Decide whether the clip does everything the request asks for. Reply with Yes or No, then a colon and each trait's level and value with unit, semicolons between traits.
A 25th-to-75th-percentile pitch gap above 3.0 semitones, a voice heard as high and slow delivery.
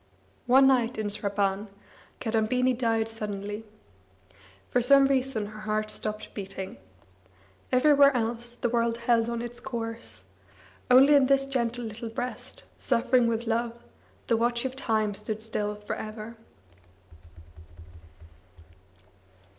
No: narrow, 2.5 semitones; high, 230 Hz; slow, 120 wpm